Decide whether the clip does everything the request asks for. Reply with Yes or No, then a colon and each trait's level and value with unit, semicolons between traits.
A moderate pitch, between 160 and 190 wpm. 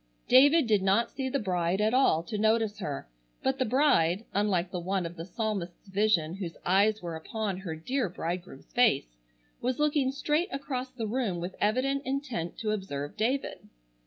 No: high, 210 Hz; average, 175 wpm